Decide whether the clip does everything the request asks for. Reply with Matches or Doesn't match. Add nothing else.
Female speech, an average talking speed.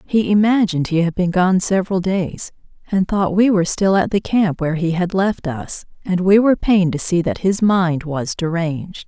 Doesn't match